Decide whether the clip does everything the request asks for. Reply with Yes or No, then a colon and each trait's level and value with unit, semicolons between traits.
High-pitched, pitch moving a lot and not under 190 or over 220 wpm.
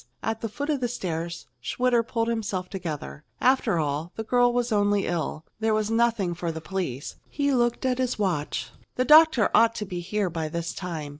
Yes: high, 210 Hz; wide, 6.0 semitones; average, 200 wpm